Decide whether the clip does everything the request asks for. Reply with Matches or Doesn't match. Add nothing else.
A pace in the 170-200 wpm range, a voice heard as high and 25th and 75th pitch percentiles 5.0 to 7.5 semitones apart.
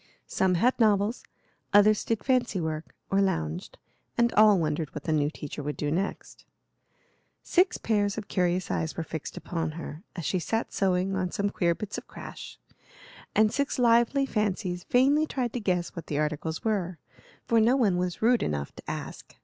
Matches